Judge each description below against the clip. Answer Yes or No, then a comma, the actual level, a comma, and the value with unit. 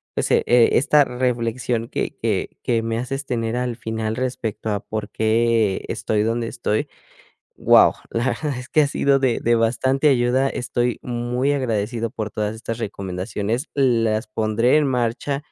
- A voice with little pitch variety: Yes, narrow, 2.3 semitones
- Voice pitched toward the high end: No, low, 120 Hz